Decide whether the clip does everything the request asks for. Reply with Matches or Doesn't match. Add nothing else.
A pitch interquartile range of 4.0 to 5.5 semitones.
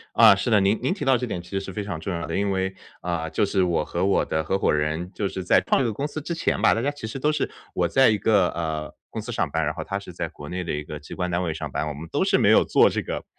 Matches